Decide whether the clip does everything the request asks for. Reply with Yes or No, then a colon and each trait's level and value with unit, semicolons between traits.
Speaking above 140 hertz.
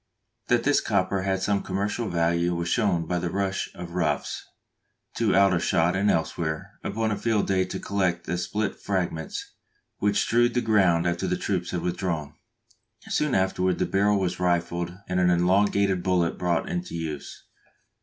No: very low, 90 Hz